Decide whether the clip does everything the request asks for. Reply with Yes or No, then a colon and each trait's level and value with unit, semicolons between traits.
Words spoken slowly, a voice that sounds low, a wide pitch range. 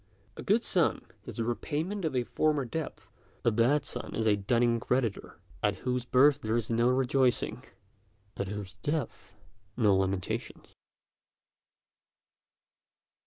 No: slow, 130 wpm; low, 120 Hz; average, 4.5 semitones